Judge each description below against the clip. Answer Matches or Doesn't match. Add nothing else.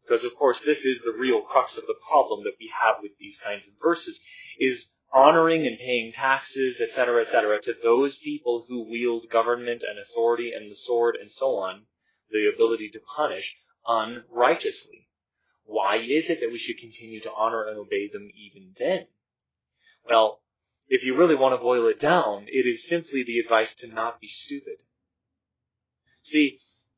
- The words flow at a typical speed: Matches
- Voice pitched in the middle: Doesn't match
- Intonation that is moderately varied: Doesn't match